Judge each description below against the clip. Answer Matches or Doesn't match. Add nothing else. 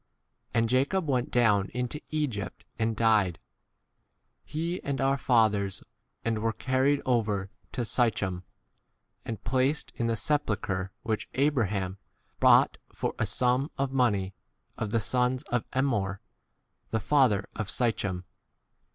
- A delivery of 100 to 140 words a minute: Matches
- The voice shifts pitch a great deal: Doesn't match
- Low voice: Matches